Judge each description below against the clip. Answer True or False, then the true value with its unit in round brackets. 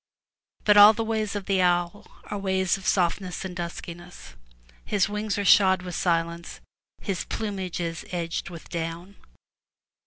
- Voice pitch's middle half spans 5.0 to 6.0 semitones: False (2.9 semitones)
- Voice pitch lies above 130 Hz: True (185 Hz)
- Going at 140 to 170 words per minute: True (150 wpm)